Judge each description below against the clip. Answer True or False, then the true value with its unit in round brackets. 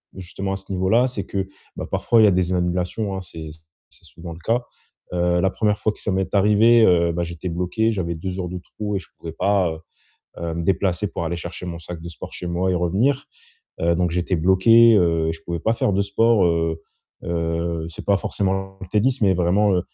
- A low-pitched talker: True (90 Hz)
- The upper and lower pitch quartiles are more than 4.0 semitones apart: False (2.9 semitones)